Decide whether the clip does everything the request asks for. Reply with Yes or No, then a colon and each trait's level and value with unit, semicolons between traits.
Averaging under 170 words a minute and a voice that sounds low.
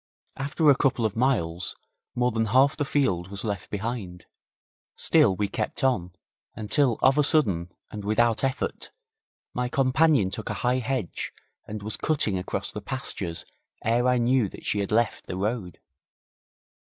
Yes: average, 160 wpm; low, 115 Hz